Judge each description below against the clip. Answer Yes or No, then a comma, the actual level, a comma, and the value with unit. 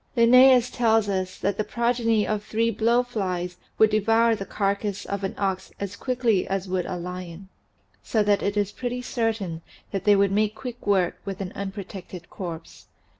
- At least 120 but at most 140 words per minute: No, average, 175 wpm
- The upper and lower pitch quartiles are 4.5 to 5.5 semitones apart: No, average, 3.1 semitones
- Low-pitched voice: No, high, 205 Hz